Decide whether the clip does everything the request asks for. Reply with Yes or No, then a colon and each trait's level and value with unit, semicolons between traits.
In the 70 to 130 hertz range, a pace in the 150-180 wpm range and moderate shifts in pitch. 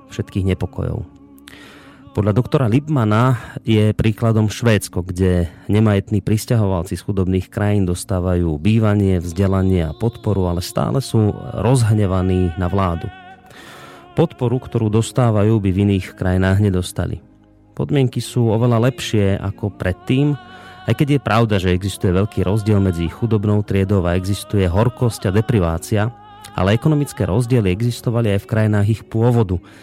No: low, 105 Hz; average, 130 wpm; average, 3.7 semitones